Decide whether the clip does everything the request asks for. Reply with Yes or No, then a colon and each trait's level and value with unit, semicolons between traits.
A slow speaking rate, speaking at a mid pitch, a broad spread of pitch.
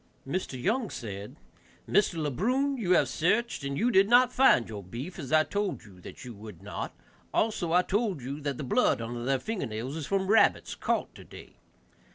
No: average, 195 wpm; medium, 155 Hz; wide, 8.8 semitones